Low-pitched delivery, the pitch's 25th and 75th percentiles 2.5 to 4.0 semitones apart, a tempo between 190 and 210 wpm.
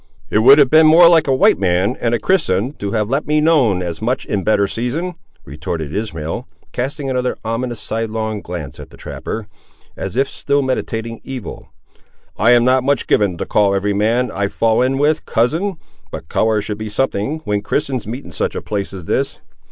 No: low, 115 Hz; average, 4.8 semitones; average, 200 wpm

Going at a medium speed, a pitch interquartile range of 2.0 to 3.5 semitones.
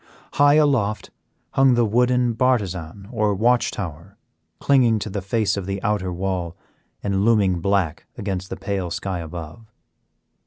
No: average, 145 wpm; average, 3.9 semitones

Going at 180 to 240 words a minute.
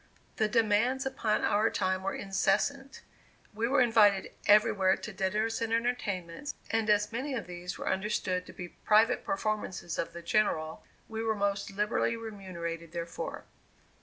No: average, 150 wpm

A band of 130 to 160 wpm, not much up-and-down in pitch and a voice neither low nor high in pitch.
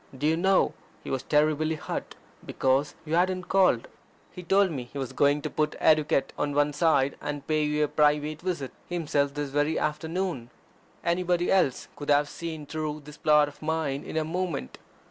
No: average, 185 wpm; narrow, 2.3 semitones; medium, 150 Hz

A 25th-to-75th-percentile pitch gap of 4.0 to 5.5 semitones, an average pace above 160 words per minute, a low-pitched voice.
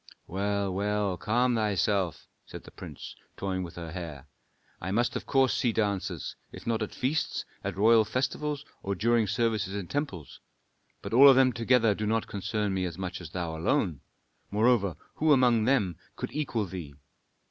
Yes: average, 4.4 semitones; average, 170 wpm; low, 105 Hz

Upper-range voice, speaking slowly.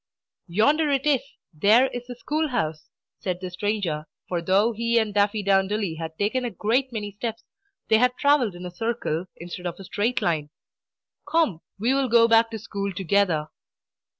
No: high, 210 Hz; average, 175 wpm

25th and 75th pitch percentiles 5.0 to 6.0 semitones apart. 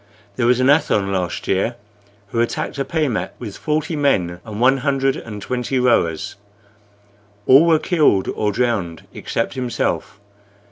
Yes: wide, 5.4 semitones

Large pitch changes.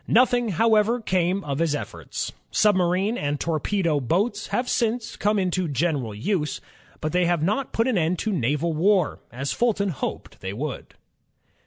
Yes: wide, 5.7 semitones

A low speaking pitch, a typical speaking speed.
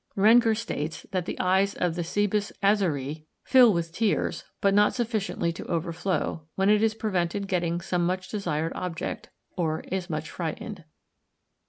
No: medium, 185 Hz; average, 155 wpm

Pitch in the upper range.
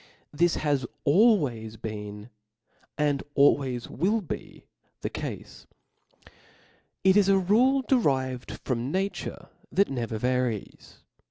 No: medium, 140 Hz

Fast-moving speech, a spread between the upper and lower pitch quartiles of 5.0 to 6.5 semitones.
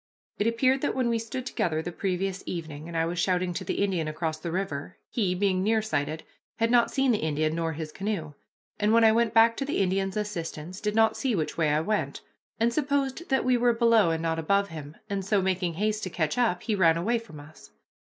Yes: fast, 230 wpm; wide, 5.6 semitones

